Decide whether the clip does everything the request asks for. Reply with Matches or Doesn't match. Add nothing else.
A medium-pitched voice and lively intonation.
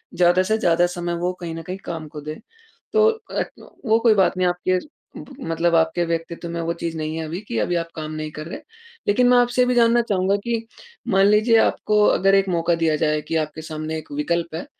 Doesn't match